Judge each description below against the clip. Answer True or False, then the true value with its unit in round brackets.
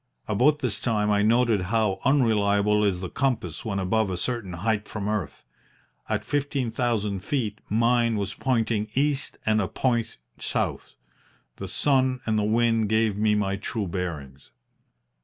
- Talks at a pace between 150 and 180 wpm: True (155 wpm)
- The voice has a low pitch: True (110 Hz)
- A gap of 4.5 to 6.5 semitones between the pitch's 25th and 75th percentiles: False (2.9 semitones)